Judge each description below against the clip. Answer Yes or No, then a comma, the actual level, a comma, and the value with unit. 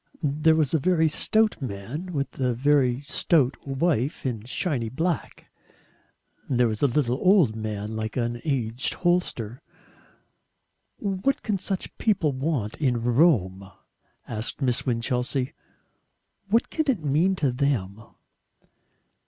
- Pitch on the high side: No, low, 135 Hz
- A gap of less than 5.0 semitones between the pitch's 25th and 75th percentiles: No, wide, 5.5 semitones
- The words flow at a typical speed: No, slow, 125 wpm